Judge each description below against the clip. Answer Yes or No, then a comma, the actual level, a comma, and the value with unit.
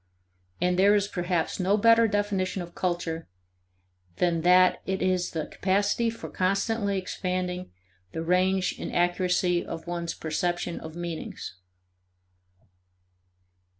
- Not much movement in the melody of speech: Yes, narrow, 2.0 semitones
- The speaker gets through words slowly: Yes, slow, 115 wpm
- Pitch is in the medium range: Yes, medium, 180 Hz